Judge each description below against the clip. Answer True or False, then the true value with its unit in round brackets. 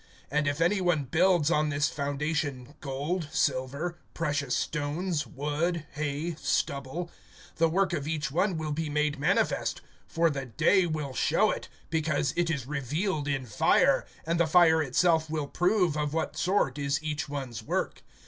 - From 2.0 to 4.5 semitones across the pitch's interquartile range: True (2.9 semitones)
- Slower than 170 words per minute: True (160 wpm)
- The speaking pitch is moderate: True (150 Hz)